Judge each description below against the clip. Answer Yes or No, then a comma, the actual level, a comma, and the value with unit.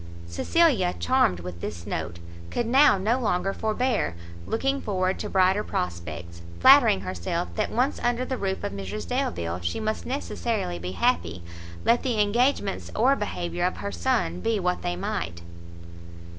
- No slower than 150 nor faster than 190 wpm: Yes, average, 155 wpm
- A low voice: No, medium, 185 Hz